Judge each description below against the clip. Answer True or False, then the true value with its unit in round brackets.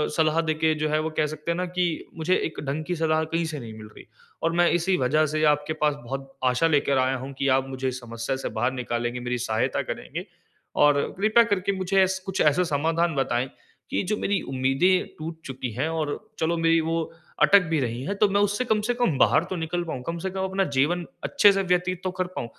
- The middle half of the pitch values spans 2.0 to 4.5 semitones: False (5.1 semitones)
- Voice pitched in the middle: True (160 Hz)